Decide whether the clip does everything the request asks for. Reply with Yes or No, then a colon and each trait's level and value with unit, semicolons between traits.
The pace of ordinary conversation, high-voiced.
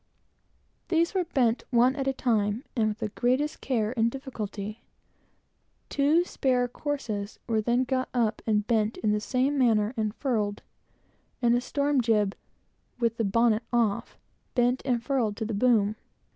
Yes: average, 160 wpm; high, 235 Hz